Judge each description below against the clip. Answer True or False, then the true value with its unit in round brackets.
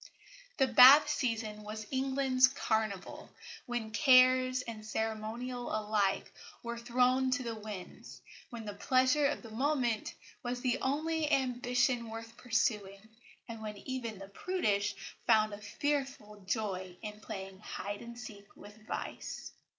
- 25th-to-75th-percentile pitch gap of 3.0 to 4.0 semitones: True (3.3 semitones)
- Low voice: False (235 Hz)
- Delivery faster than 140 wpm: False (135 wpm)